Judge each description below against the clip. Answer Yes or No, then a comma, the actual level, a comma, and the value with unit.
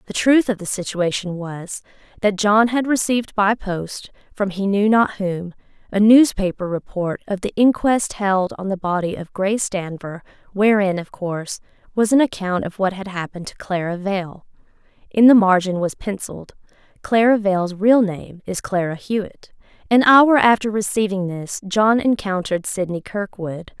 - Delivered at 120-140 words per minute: No, average, 160 wpm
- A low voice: No, high, 200 Hz